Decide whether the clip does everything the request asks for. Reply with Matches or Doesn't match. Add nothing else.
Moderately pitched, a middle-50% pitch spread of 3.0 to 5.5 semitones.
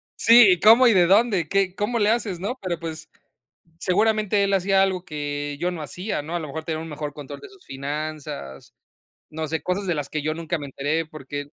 Matches